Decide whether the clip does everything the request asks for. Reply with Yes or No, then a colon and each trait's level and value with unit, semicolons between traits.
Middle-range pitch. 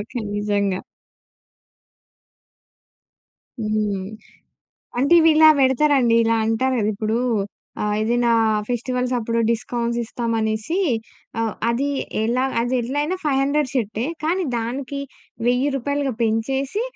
No: high, 240 Hz